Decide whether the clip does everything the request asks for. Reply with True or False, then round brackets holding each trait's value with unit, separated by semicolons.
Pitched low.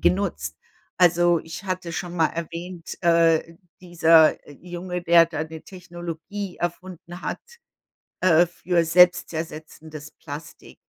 False (170 Hz)